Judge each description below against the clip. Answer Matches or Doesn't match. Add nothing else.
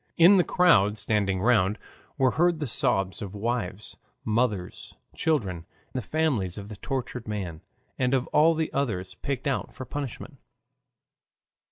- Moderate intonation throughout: Doesn't match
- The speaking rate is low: Doesn't match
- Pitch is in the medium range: Doesn't match